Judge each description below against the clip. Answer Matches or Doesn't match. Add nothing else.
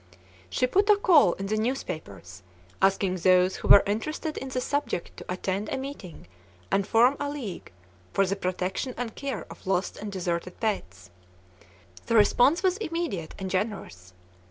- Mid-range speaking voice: Doesn't match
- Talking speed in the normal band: Matches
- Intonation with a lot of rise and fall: Matches